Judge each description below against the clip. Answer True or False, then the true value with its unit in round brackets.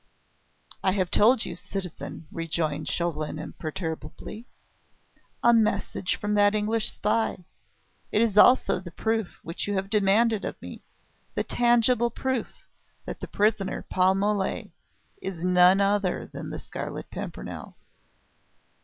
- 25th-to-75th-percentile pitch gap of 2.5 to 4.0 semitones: True (3.5 semitones)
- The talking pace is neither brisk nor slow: False (125 wpm)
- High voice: True (200 Hz)